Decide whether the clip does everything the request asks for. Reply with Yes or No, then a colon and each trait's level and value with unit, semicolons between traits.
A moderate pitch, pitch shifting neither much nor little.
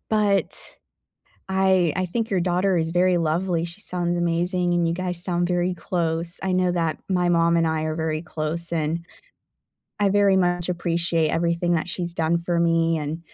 No: medium, 175 Hz; narrow, 1.5 semitones